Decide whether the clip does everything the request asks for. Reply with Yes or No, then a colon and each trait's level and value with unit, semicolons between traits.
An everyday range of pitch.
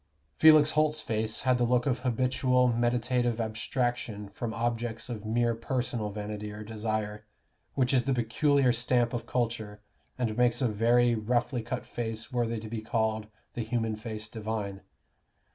No: narrow, 2.2 semitones